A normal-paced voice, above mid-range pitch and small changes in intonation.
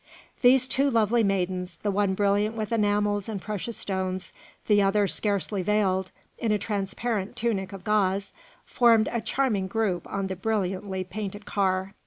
Yes: average, 155 wpm; high, 205 Hz; narrow, 2.2 semitones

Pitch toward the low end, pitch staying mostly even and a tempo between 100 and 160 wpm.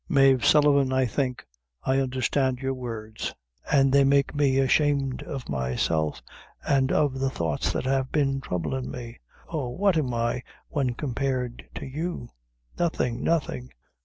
Yes: low, 130 Hz; narrow, 2.2 semitones; average, 145 wpm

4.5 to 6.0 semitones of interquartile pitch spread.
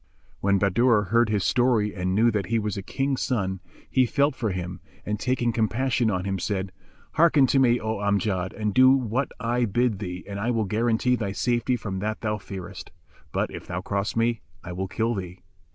No: average, 3.6 semitones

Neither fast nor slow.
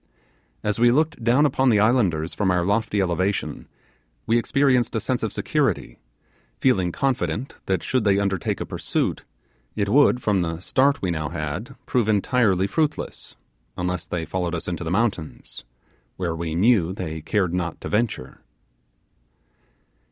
Yes: average, 150 wpm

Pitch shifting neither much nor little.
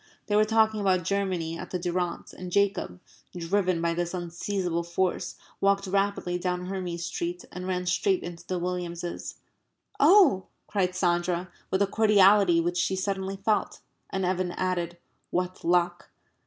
No: narrow, 2.1 semitones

